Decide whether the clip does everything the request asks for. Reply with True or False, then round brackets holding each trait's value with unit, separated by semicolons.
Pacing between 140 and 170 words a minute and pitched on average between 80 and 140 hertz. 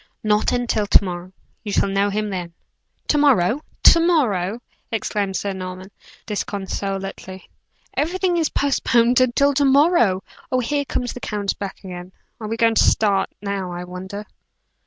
False (155 wpm; 210 Hz)